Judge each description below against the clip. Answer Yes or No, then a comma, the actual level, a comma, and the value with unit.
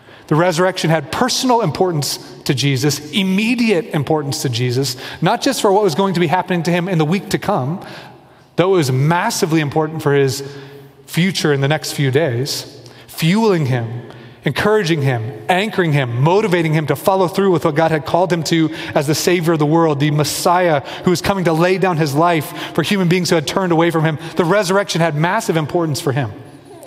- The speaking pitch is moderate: Yes, medium, 165 Hz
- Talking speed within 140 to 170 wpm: No, average, 200 wpm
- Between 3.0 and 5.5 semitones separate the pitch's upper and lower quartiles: Yes, average, 4.2 semitones